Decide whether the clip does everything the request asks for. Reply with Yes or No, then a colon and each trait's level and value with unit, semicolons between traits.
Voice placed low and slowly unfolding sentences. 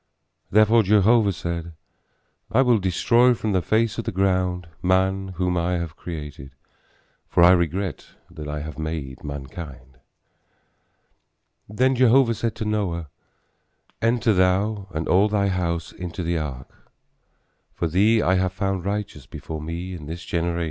No: very low, 90 Hz; average, 145 wpm